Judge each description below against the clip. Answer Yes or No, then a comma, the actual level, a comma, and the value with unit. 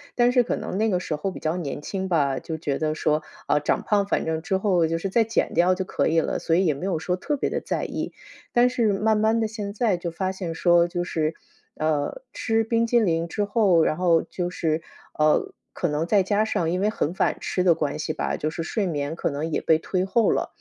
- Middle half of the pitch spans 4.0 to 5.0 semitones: Yes, average, 4.4 semitones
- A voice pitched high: No, medium, 180 Hz